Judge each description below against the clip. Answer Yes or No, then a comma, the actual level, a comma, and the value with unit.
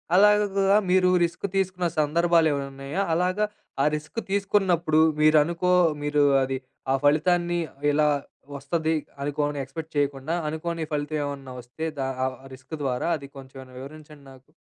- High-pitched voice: No, medium, 155 Hz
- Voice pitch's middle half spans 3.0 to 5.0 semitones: Yes, average, 3.7 semitones